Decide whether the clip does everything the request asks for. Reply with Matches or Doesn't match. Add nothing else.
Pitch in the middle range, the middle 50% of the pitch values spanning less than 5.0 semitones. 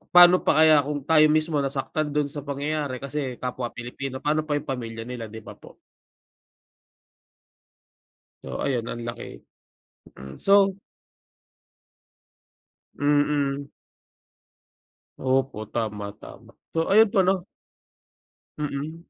Matches